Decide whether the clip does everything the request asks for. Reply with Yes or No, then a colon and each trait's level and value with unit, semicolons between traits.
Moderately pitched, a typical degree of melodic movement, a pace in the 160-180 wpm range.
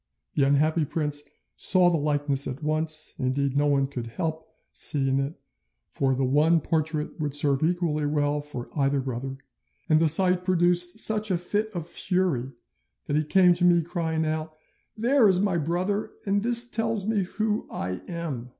Yes: medium, 155 Hz; average, 4.0 semitones; average, 170 wpm